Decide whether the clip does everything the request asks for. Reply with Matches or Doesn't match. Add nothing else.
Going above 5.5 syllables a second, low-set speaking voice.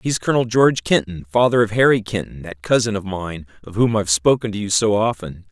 Matches